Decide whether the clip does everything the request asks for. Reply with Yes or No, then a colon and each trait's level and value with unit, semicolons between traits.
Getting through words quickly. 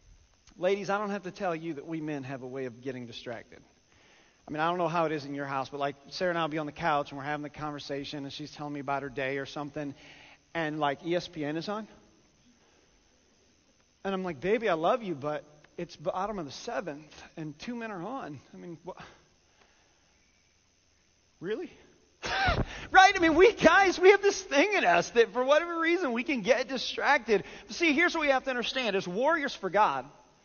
Yes: fast, 215 wpm